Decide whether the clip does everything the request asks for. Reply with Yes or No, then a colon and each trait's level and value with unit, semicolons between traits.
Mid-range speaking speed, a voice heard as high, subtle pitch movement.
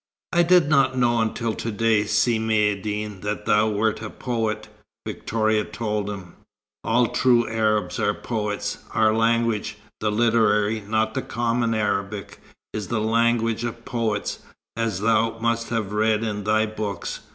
No: average, 150 wpm; low, 110 Hz; narrow, 1.6 semitones